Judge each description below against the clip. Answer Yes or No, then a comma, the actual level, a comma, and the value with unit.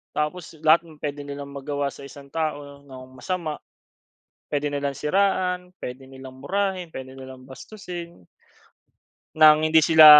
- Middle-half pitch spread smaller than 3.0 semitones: No, average, 3.4 semitones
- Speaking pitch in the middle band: Yes, medium, 150 Hz